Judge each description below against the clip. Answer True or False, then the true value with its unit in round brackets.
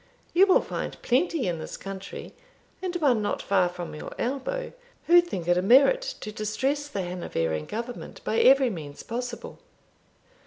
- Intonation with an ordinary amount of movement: False (8.1 semitones)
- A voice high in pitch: True (235 Hz)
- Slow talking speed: False (160 wpm)